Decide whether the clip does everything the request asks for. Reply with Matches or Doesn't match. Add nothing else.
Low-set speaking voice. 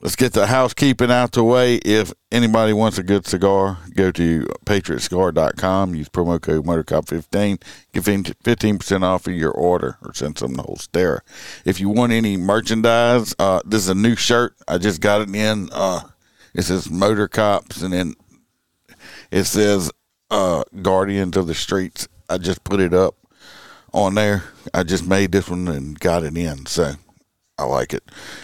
Matches